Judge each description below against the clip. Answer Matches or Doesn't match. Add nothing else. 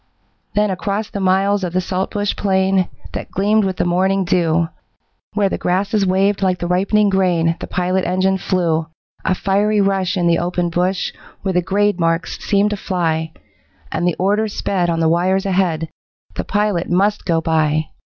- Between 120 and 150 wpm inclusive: Doesn't match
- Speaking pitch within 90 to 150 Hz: Doesn't match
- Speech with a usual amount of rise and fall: Doesn't match